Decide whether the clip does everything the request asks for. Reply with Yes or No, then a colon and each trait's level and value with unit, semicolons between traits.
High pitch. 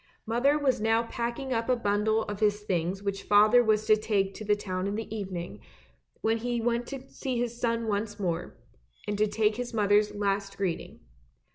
Yes: high, 215 Hz